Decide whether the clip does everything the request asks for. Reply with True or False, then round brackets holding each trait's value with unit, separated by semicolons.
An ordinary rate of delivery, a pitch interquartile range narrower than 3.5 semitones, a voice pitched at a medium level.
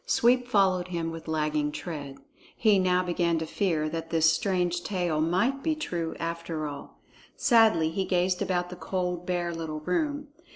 True (165 wpm; 2.7 semitones; 175 Hz)